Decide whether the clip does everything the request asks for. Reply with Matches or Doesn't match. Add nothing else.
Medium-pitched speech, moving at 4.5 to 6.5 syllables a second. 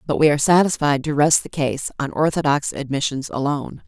Matches